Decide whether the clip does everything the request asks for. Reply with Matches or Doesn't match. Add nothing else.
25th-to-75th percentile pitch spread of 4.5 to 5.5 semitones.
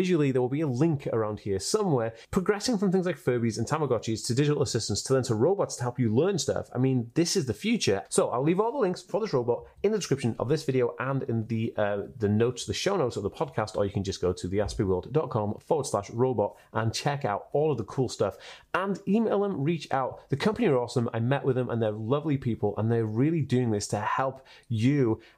Matches